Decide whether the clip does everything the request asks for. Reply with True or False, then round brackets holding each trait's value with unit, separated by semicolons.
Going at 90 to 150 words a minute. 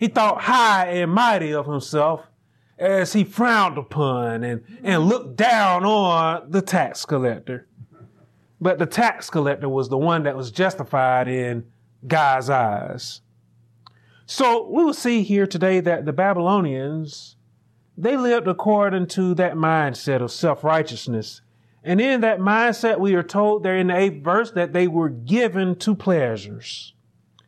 True (145 wpm)